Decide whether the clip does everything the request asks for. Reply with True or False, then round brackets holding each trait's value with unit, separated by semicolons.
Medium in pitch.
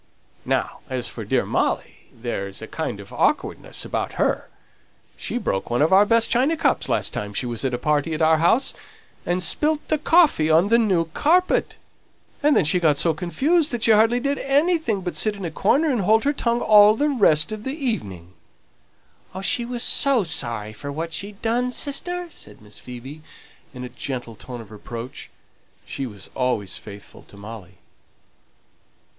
True (180 Hz)